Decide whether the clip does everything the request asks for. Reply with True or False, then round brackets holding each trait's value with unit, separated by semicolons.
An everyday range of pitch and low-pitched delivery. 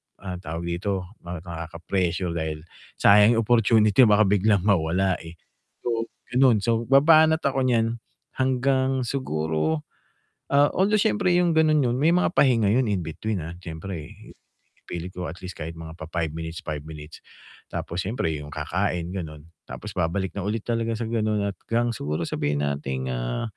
False (6.4 semitones; 100 Hz)